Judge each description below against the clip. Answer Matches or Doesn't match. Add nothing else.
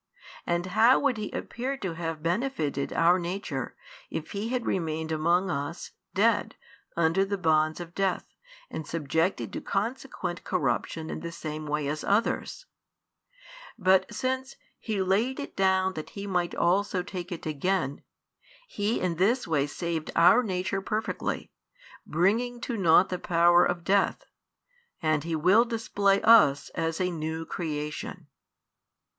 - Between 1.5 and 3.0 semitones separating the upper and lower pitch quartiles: Doesn't match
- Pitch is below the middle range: Doesn't match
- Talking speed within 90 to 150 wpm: Matches